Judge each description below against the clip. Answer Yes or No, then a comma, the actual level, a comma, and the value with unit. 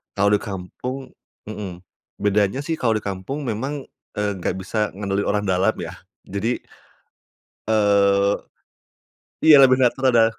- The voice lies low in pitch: Yes, low, 105 Hz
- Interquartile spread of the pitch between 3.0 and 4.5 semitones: Yes, average, 4.2 semitones